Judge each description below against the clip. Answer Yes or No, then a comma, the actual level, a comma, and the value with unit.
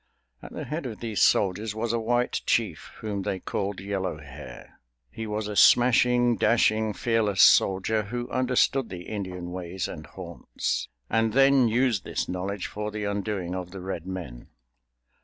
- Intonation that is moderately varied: Yes, average, 3.9 semitones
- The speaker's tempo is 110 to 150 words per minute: No, average, 160 wpm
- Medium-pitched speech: No, low, 105 Hz